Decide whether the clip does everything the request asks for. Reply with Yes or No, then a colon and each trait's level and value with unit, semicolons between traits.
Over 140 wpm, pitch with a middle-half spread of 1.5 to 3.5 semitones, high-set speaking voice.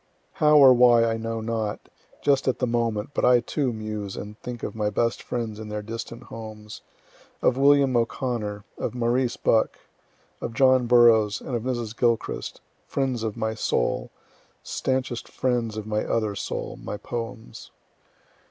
No: average, 160 wpm; narrow, 2.4 semitones; low, 115 Hz